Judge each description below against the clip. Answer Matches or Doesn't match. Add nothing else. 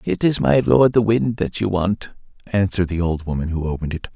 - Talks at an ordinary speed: Doesn't match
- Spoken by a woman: Doesn't match